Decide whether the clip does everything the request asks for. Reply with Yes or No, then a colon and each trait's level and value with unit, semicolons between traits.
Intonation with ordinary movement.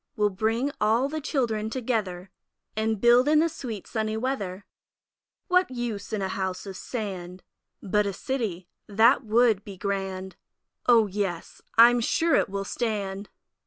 Yes: average, 3.8 semitones